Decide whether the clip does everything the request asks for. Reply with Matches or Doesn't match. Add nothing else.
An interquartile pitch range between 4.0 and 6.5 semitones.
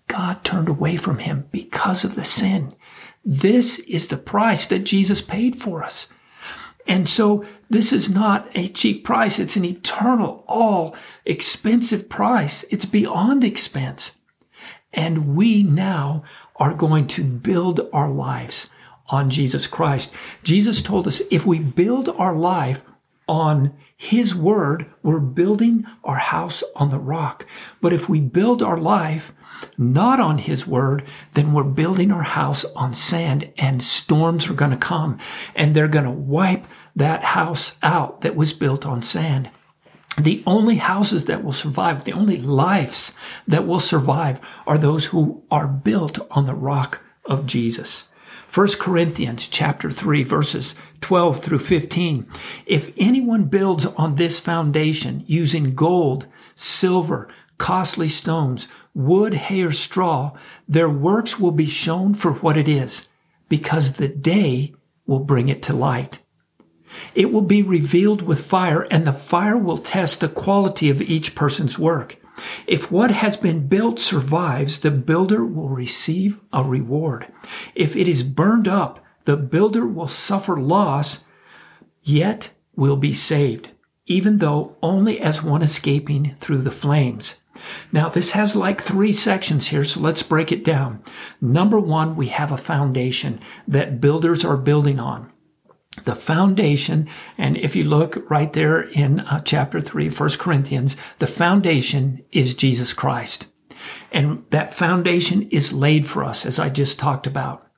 Matches